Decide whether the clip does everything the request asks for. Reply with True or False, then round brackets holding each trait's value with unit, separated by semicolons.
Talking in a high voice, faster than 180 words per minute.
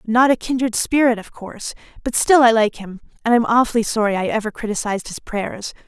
True (225 Hz; 205 wpm)